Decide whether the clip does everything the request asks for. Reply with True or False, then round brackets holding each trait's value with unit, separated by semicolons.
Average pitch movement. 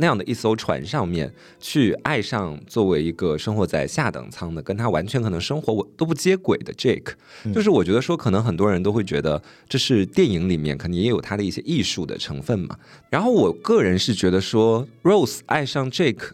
False (6.7 semitones)